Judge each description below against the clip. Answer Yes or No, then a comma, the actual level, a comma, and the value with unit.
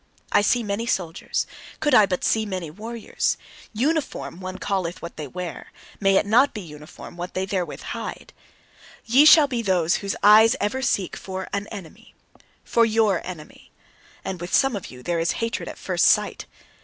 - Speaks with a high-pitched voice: Yes, high, 200 Hz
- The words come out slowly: No, average, 180 wpm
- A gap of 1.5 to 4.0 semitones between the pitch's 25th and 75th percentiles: No, average, 4.5 semitones